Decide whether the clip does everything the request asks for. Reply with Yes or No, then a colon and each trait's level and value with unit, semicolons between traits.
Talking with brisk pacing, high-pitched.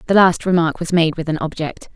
No: fast, 245 wpm; medium, 165 Hz